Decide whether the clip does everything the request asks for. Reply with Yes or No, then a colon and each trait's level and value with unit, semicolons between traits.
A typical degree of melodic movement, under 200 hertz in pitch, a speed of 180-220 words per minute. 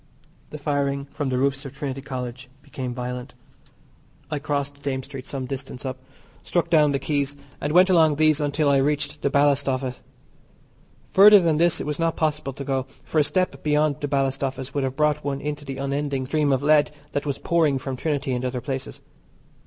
No: narrow, 2.0 semitones; medium, 140 Hz; average, 200 wpm